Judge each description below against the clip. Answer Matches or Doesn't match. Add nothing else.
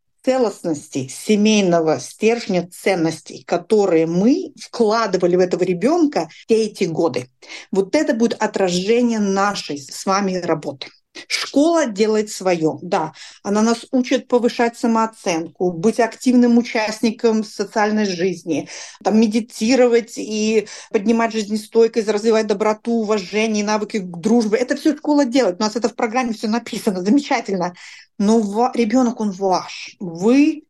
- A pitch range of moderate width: Matches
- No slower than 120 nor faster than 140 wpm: Matches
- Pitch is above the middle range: Matches